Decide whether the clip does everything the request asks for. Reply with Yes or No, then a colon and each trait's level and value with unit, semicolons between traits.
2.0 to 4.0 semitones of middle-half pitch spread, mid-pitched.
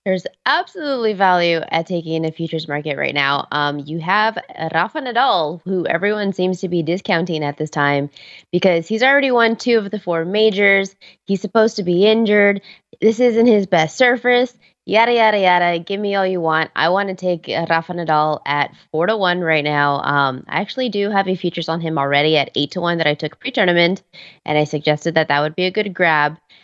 No: average, 4.5 semitones; medium, 175 Hz